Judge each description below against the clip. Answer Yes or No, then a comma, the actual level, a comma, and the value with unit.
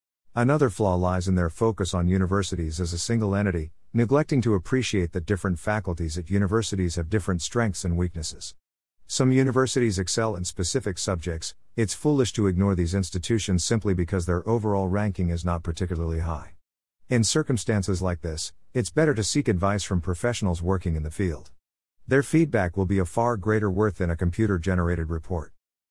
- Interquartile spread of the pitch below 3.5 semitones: No, average, 4.2 semitones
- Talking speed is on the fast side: No, average, 170 wpm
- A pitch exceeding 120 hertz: No, very low, 95 Hz